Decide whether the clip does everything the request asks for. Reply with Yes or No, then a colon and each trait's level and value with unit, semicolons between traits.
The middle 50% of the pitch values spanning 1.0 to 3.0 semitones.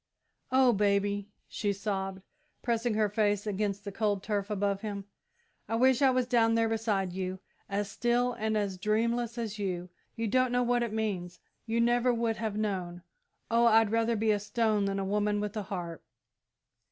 Yes: narrow, 2.5 semitones